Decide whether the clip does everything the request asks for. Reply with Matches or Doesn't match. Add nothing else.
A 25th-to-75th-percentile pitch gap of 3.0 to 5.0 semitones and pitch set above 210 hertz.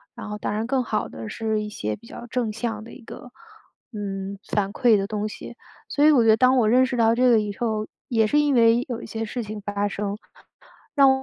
Doesn't match